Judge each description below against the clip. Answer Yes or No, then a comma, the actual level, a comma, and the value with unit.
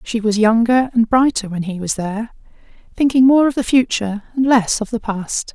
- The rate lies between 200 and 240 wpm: Yes, fast, 205 wpm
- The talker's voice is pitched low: No, high, 230 Hz